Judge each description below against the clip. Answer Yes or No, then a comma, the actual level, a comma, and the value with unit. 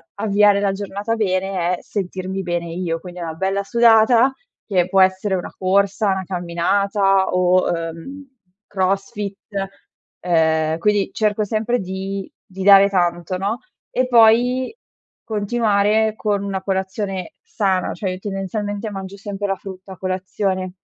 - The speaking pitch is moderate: No, high, 195 Hz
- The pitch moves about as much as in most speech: No, narrow, 1.9 semitones